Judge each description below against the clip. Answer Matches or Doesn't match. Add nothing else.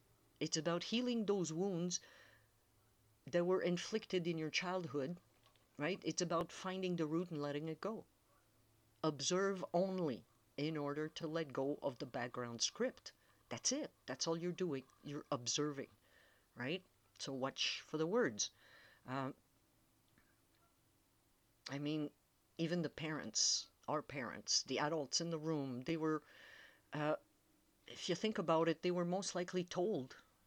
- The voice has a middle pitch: Matches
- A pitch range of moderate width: Matches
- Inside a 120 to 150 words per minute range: Matches